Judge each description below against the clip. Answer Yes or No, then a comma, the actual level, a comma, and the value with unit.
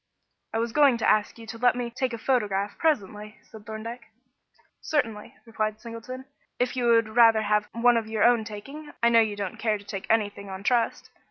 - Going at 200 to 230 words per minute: Yes, fast, 205 wpm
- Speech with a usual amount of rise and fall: No, narrow, 2.3 semitones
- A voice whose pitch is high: Yes, high, 225 Hz